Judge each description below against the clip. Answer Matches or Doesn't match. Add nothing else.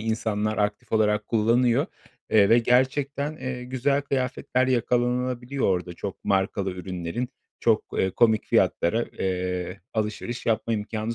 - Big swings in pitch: Doesn't match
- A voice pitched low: Matches